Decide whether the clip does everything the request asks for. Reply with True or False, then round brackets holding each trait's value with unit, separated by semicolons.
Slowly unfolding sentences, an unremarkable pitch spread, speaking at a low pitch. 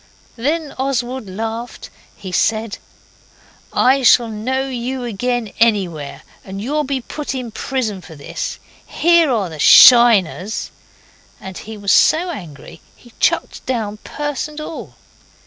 False (130 wpm; 4.5 semitones; 235 Hz)